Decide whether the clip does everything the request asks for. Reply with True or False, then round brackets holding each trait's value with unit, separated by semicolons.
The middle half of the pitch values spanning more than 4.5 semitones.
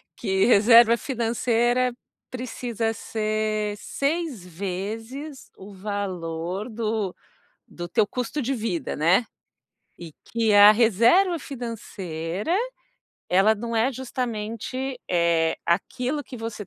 False (4.0 semitones)